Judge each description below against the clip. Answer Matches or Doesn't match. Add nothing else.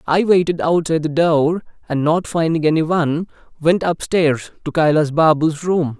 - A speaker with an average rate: Matches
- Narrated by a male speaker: Matches